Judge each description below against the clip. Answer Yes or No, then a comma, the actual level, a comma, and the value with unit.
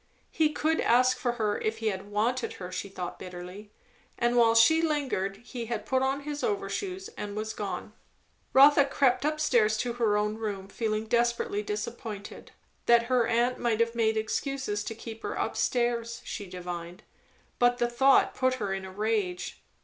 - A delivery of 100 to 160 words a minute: No, average, 180 wpm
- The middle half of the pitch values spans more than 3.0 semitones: Yes, average, 3.5 semitones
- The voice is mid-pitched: No, high, 230 Hz